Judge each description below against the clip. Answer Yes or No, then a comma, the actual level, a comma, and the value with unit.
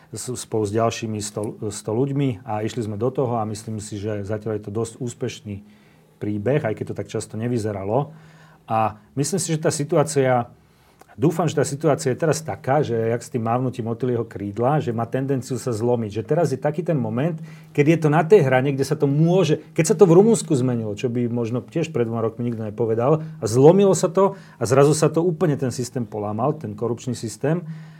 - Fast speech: Yes, fast, 210 wpm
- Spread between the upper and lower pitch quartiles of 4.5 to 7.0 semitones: Yes, average, 5.3 semitones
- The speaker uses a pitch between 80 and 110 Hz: No, low, 125 Hz